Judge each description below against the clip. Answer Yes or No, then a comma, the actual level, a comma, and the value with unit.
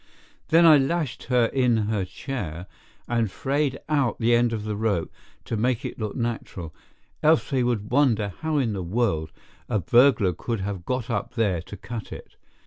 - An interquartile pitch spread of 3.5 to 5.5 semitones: Yes, average, 4.4 semitones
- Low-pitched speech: Yes, low, 115 Hz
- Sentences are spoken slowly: No, average, 180 wpm